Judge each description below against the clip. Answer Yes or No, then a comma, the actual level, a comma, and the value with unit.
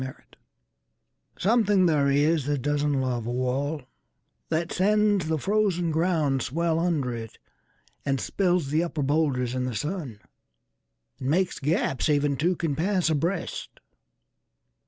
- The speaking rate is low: Yes, slow, 125 wpm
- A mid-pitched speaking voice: Yes, medium, 150 Hz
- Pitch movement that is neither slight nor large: Yes, average, 4.7 semitones